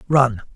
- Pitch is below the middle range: Yes, low, 125 Hz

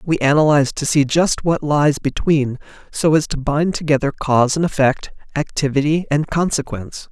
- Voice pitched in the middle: Yes, medium, 145 Hz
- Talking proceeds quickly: No, average, 160 wpm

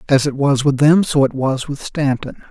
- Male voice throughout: Yes, male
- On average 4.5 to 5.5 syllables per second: Yes, 5.0 syllables/s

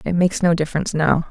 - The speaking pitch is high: No, medium, 170 Hz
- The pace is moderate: No, fast, 230 wpm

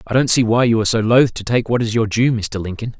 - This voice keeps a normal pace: No, fast, 320 wpm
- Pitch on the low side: Yes, low, 115 Hz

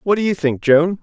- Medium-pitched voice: Yes, medium, 170 Hz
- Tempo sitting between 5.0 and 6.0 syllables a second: Yes, 5.4 syllables/s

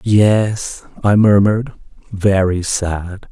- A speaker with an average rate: No, slow, 90 wpm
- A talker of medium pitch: No, low, 100 Hz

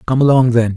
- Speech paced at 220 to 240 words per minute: Yes, fast, 235 wpm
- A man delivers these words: Yes, male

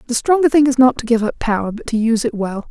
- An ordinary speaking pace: No, fast, 310 wpm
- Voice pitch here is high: Yes, high, 240 Hz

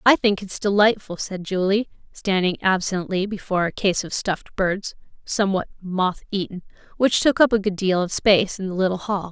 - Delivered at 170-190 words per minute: Yes, average, 185 wpm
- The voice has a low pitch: No, high, 195 Hz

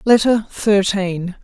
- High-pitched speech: Yes, high, 200 Hz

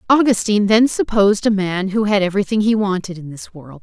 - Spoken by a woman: Yes, female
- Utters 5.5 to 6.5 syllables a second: Yes, 6.0 syllables/s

